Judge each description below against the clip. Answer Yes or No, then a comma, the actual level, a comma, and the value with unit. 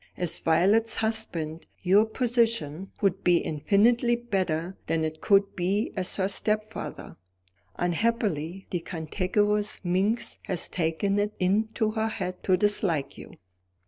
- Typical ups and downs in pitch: Yes, average, 3.7 semitones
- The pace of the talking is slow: Yes, slow, 125 wpm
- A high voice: Yes, high, 195 Hz